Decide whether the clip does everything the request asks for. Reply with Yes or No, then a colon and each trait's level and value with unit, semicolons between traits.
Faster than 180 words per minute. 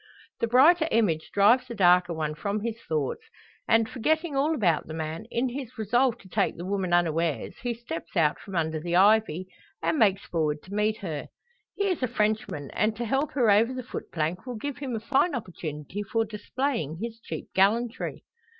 Yes: average, 190 wpm